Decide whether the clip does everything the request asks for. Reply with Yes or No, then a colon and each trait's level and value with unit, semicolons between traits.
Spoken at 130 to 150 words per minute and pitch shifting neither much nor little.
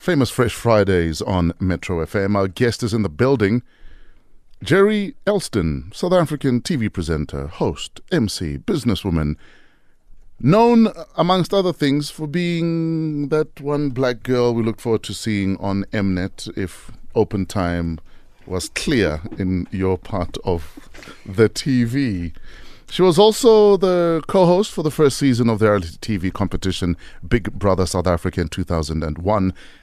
No: average, 145 wpm; wide, 8.2 semitones